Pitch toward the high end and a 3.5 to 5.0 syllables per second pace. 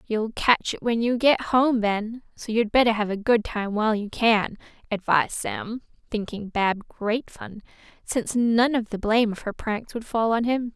Yes: high, 225 Hz; 4.5 syllables/s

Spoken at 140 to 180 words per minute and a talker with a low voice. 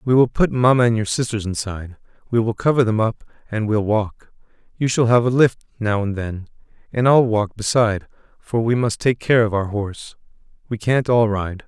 No: fast, 205 wpm; low, 110 Hz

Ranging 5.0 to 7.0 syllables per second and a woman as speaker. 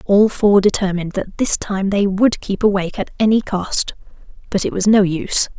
Yes: 5.2 syllables/s; female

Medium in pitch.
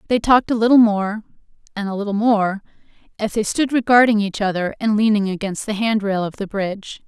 No: high, 210 Hz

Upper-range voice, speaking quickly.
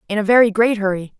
Yes: high, 210 Hz; fast, 250 wpm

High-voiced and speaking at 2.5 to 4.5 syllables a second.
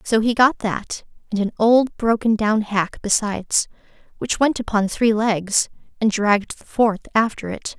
Yes: high, 215 Hz; 4.4 syllables/s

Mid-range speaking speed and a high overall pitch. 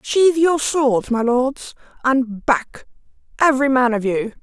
Yes: average, 150 wpm; very high, 260 Hz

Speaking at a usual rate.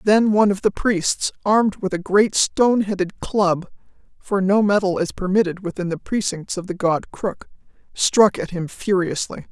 Yes: average, 165 wpm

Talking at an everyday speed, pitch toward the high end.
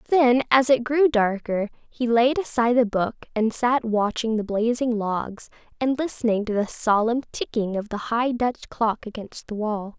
Yes: average, 180 wpm; high, 230 Hz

